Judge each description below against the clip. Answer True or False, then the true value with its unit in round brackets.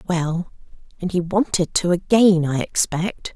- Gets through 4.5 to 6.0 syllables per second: False (4.1 syllables/s)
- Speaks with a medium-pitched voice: True (175 Hz)